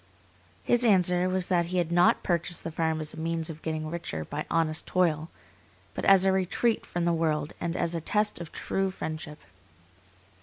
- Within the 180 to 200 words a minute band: Yes, average, 190 wpm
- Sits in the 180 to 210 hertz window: No, medium, 170 Hz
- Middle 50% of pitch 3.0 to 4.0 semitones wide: No, narrow, 2.4 semitones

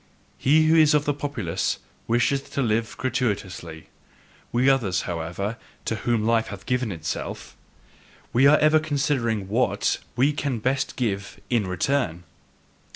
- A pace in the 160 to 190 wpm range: No, average, 140 wpm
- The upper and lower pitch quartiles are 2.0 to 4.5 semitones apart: No, wide, 5.6 semitones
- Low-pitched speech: Yes, low, 120 Hz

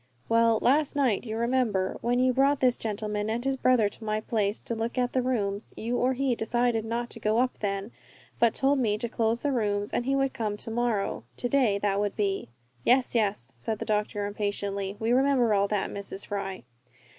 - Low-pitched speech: No, high, 225 Hz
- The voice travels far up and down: No, average, 3.2 semitones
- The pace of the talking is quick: Yes, fast, 210 wpm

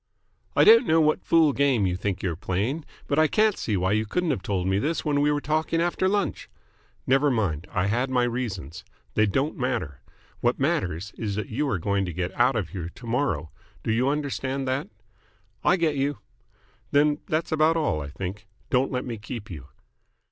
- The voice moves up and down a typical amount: No, wide, 7.1 semitones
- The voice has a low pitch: Yes, low, 125 Hz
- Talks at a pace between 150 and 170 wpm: No, average, 200 wpm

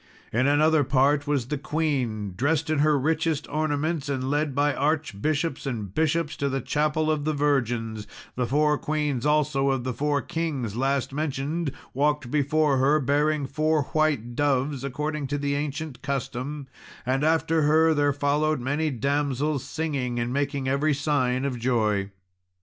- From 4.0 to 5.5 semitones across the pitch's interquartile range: No, narrow, 2.5 semitones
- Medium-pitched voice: Yes, medium, 145 Hz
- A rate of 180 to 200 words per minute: No, average, 155 wpm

